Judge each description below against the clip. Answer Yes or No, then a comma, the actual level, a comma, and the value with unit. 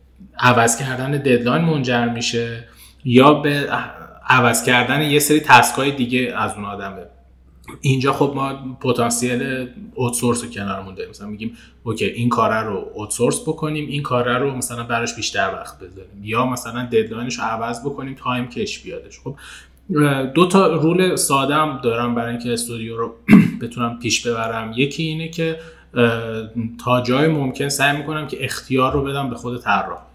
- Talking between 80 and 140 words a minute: No, fast, 155 wpm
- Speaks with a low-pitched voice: Yes, low, 125 Hz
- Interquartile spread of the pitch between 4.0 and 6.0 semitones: No, average, 3.2 semitones